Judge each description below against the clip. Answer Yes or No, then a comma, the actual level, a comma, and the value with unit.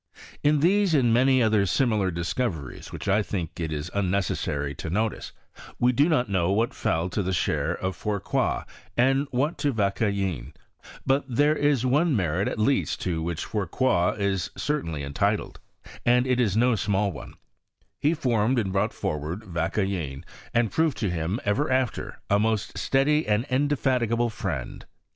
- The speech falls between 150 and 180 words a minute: Yes, average, 155 wpm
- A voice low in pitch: Yes, low, 105 Hz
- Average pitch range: No, wide, 6.3 semitones